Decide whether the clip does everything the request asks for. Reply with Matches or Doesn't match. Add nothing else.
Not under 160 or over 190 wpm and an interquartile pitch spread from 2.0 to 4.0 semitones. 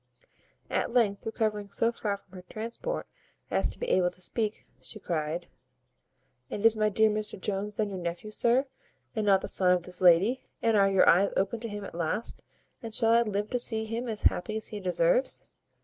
Doesn't match